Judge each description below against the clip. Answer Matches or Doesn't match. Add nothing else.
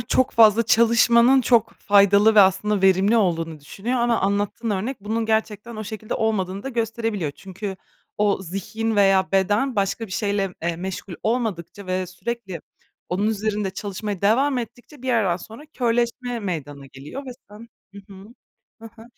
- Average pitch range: Matches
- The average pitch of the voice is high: Matches